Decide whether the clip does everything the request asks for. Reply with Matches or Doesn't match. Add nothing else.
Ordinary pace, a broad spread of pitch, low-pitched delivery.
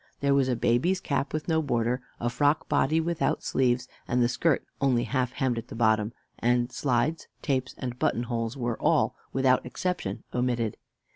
Doesn't match